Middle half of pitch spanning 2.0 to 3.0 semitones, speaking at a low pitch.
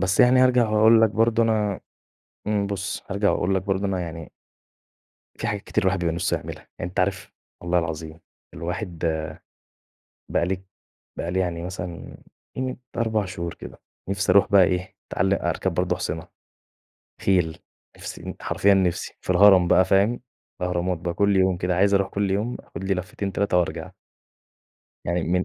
Yes: narrow, 2.4 semitones; very low, 95 Hz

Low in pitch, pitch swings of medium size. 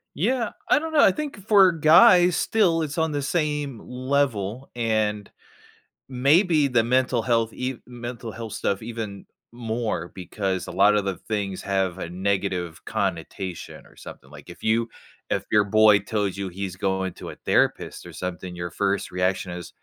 No: low, 110 Hz; wide, 6.4 semitones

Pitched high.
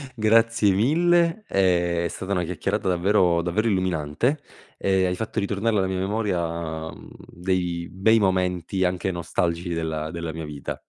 No: very low, 90 Hz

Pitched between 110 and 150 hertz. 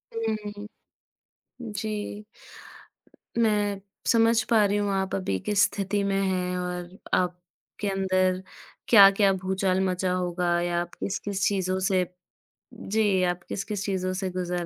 No: high, 190 Hz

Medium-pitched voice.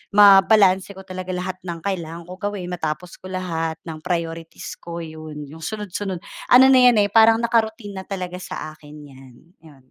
Yes: medium, 180 Hz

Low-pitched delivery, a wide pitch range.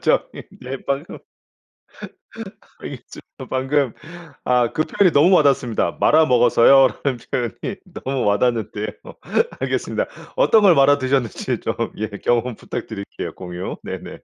No: low, 130 Hz; average, 3.4 semitones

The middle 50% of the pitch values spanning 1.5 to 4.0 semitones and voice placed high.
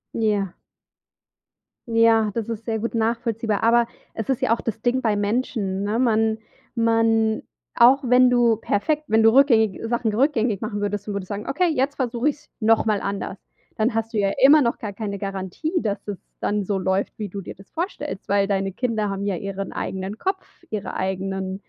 Yes: average, 2.8 semitones; high, 220 Hz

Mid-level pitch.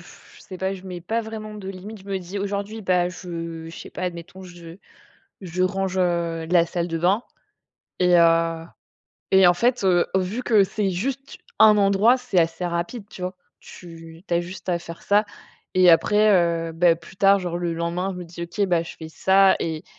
Yes: medium, 180 Hz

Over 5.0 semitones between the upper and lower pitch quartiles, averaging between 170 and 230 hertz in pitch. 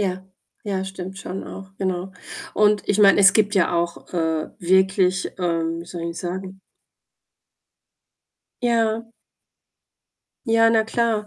No: average, 2.8 semitones; high, 190 Hz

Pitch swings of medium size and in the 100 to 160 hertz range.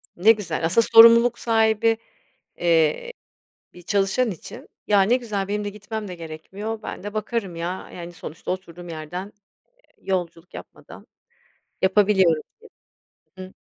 No: average, 4.0 semitones; high, 195 Hz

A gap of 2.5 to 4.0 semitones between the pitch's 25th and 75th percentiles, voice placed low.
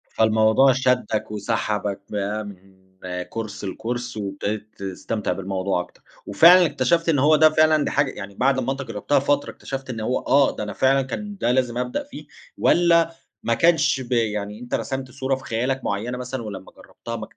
No: average, 4.6 semitones; low, 125 Hz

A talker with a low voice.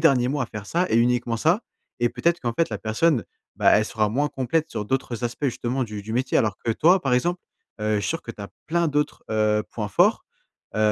Yes: low, 120 Hz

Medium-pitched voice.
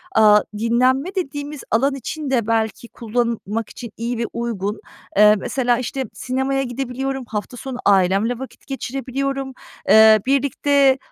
No: high, 245 Hz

